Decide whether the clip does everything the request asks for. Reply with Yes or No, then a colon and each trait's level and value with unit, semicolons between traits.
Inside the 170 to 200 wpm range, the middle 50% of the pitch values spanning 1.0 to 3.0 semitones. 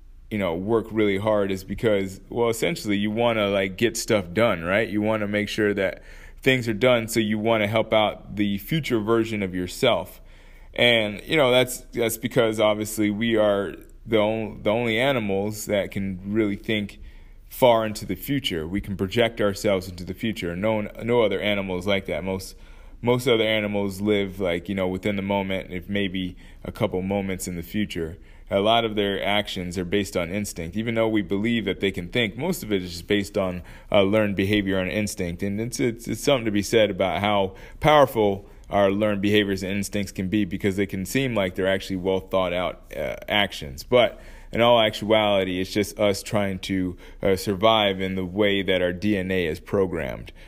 Yes: average, 195 wpm; narrow, 2.4 semitones